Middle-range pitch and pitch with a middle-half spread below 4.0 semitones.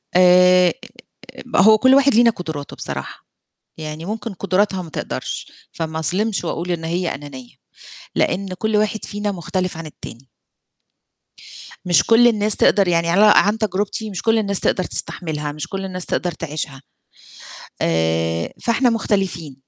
No: medium, 180 Hz; average, 4.8 semitones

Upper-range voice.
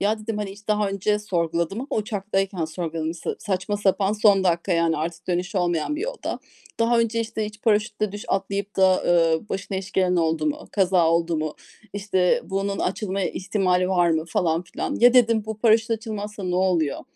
Yes: high, 195 Hz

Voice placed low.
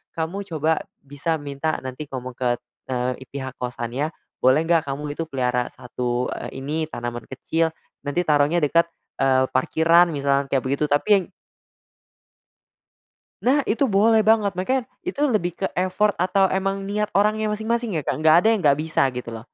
No: medium, 155 Hz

